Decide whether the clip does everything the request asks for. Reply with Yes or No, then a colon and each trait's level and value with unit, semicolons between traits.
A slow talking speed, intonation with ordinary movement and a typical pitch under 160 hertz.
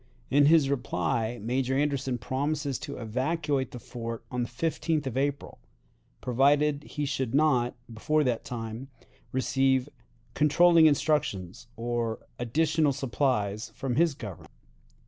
Yes: slow, 125 wpm; average, 3.6 semitones; low, 135 Hz